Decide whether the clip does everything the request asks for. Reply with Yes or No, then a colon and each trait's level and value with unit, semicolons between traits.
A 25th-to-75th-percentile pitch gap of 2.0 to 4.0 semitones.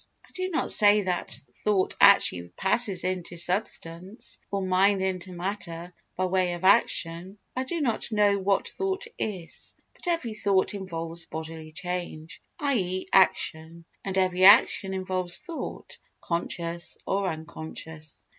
Yes: average, 2.9 semitones